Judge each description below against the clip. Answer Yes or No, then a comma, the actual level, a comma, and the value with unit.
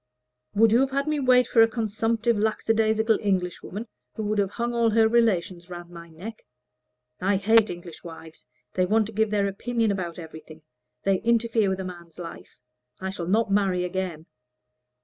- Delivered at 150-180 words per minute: Yes, average, 175 wpm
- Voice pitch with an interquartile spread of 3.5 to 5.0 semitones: Yes, average, 3.9 semitones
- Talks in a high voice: Yes, high, 205 Hz